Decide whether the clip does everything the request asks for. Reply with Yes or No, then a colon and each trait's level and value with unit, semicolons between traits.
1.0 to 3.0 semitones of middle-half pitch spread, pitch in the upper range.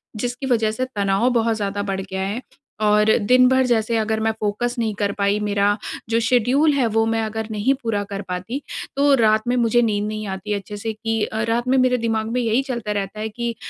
Yes: narrow, 2.5 semitones; high, 220 Hz